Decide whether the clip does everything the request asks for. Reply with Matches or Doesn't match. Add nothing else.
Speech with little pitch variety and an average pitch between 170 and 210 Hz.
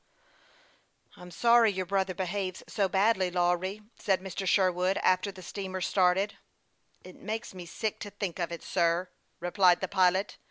Matches